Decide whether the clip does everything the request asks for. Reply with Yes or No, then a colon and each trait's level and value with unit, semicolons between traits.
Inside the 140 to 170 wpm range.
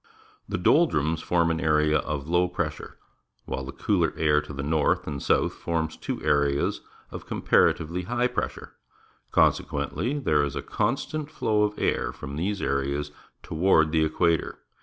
Yes: average, 160 wpm